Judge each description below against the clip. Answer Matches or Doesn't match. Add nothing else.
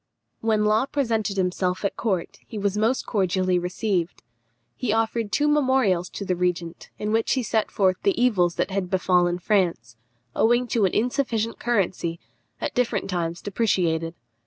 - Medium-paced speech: Matches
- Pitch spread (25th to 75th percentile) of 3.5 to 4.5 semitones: Matches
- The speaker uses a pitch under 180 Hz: Doesn't match